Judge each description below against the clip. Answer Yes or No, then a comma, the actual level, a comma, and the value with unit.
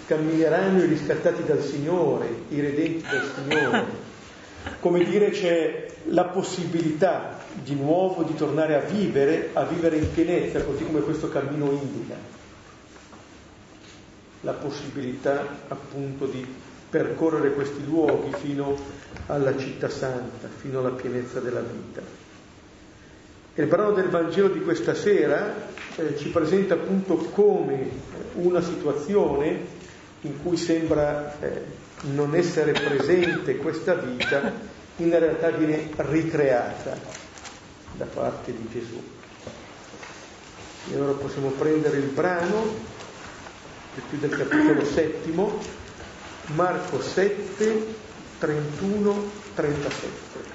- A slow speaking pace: Yes, slow, 110 wpm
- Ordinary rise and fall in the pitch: Yes, average, 3.7 semitones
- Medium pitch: Yes, medium, 155 Hz